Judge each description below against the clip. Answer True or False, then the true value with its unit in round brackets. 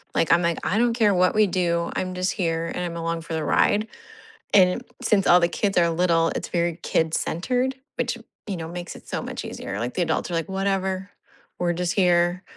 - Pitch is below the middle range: False (175 Hz)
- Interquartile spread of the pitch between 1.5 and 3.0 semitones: True (2.4 semitones)